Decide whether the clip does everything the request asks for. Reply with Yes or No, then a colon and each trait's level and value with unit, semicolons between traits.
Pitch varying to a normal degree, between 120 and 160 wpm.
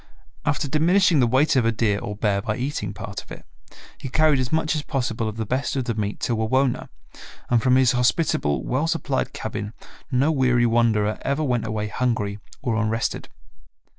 No: average, 3.9 semitones; average, 190 wpm